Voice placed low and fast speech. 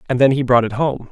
Yes: low, 125 Hz; fast, 325 wpm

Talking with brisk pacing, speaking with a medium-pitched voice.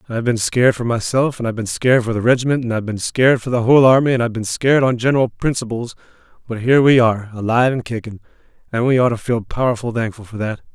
No: fast, 240 wpm; low, 120 Hz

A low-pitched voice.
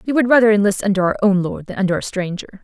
No: high, 200 Hz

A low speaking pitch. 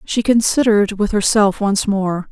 No: high, 205 Hz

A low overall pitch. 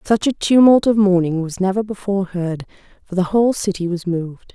No: high, 190 Hz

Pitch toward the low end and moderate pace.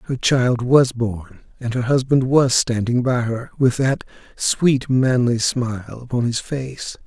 Yes: low, 125 Hz; average, 160 wpm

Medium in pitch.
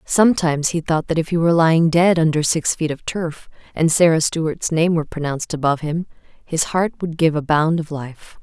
Yes: medium, 160 Hz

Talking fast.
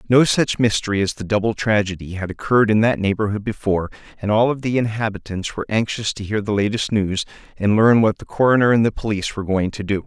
Yes: fast, 220 wpm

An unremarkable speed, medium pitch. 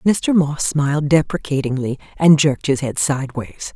Yes: average, 145 wpm; medium, 145 Hz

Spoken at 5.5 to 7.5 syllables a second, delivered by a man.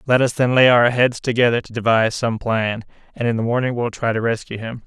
Yes: 6.0 syllables/s; male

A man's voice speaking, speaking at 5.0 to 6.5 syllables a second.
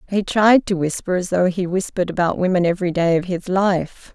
No: female; 5.5 syllables/s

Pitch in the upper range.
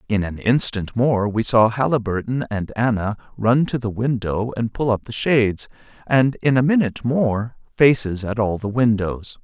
No: low, 115 Hz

